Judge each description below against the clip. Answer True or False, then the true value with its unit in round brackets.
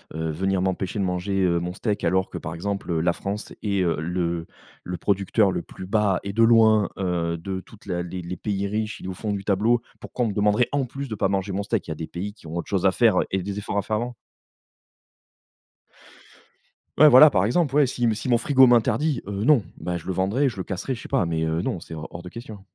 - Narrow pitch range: False (3.6 semitones)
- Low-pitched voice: True (100 Hz)